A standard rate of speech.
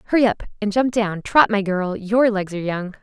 No: fast, 240 wpm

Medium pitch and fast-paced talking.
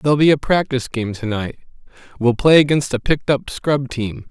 No: low, 130 Hz; fast, 210 wpm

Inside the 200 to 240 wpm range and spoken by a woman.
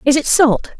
Yes: fast, 225 wpm; female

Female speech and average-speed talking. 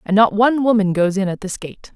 No: female; fast, 275 wpm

